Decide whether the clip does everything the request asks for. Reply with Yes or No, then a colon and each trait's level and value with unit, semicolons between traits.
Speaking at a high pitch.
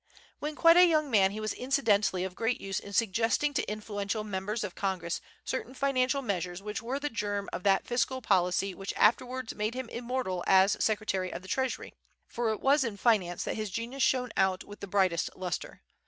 Yes: high, 215 Hz